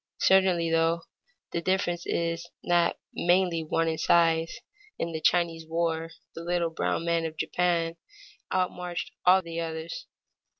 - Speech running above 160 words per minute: No, slow, 135 wpm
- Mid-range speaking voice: Yes, medium, 170 Hz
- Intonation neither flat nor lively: No, narrow, 1.1 semitones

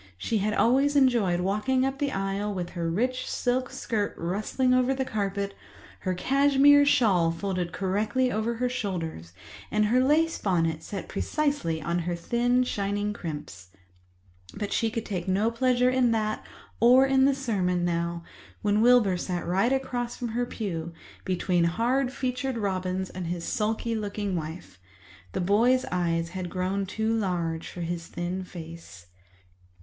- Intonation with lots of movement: Yes, wide, 5.9 semitones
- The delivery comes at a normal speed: Yes, average, 155 wpm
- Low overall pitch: No, high, 205 Hz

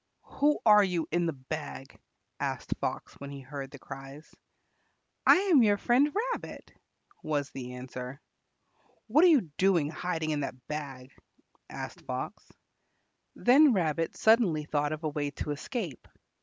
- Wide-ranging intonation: Yes, wide, 6.8 semitones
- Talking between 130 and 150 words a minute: Yes, average, 145 wpm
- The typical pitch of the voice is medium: Yes, medium, 155 Hz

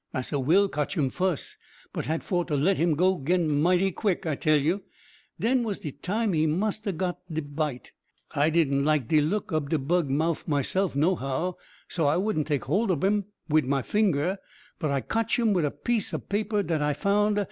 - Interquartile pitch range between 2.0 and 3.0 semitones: No, average, 4.9 semitones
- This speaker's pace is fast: Yes, fast, 210 wpm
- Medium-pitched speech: Yes, medium, 165 Hz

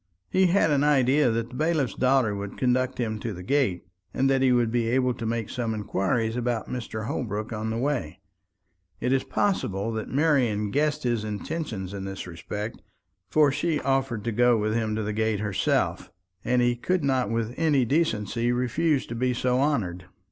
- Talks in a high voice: No, low, 120 Hz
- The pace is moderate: Yes, average, 190 wpm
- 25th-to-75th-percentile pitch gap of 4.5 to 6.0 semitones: No, average, 3.8 semitones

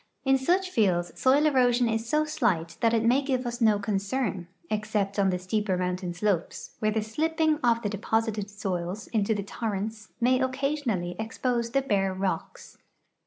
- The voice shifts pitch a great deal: No, average, 4.4 semitones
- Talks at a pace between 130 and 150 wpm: No, average, 165 wpm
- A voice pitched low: No, high, 220 Hz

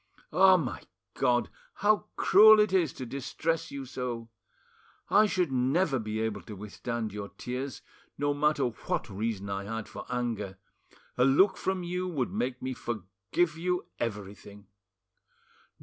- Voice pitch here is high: No, low, 125 Hz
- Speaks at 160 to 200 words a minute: No, average, 145 wpm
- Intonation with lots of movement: Yes, wide, 7.6 semitones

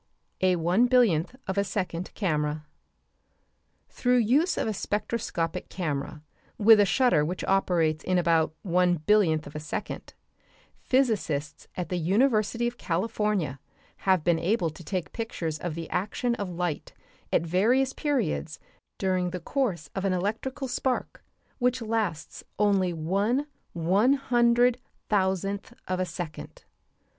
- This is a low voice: No, high, 190 Hz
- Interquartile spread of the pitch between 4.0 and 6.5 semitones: Yes, wide, 5.4 semitones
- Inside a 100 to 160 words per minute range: Yes, slow, 135 wpm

